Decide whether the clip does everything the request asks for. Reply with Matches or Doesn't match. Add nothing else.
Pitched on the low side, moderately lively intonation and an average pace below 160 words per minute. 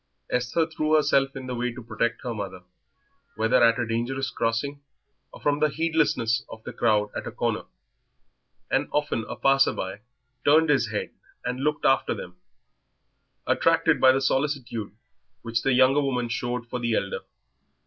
Doesn't match